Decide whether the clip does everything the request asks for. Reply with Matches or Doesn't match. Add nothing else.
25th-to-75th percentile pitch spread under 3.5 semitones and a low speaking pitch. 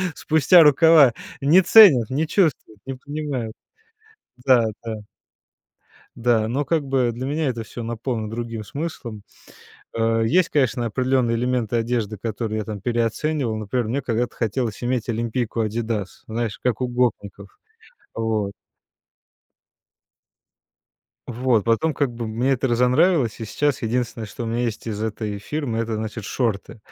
Matches